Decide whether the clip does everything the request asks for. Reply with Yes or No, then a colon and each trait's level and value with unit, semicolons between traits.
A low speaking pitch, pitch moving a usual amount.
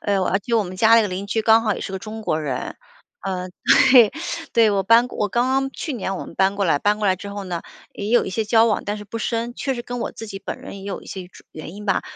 No: high, 205 Hz; average, 3.0 semitones